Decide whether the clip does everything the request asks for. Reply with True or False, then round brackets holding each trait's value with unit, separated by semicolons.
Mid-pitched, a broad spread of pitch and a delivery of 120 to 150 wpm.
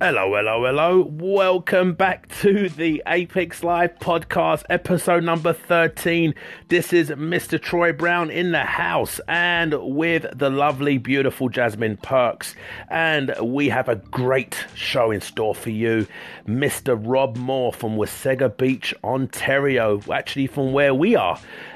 False (150 Hz; 4.8 semitones; 140 wpm)